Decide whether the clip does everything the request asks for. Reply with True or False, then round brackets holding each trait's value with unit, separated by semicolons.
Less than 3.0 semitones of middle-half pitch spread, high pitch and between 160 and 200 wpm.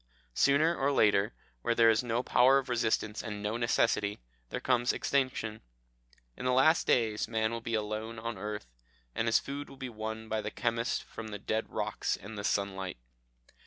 False (2.4 semitones; 115 Hz; 190 wpm)